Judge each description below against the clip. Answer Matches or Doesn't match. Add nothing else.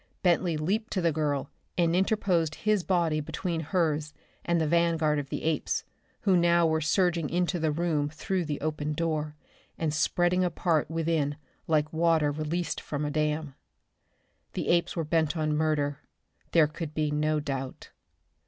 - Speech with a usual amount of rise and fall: Doesn't match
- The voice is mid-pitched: Matches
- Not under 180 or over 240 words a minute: Doesn't match